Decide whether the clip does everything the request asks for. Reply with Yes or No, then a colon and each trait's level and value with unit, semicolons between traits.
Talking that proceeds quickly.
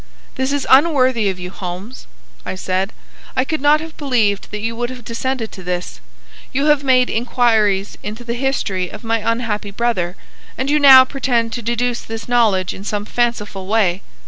No: average, 180 wpm